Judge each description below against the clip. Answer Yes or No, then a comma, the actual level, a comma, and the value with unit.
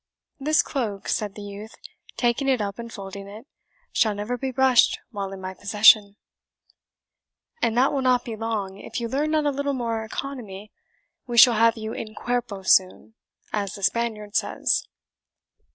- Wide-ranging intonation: No, average, 3.4 semitones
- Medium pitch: No, high, 225 Hz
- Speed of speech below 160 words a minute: No, average, 170 wpm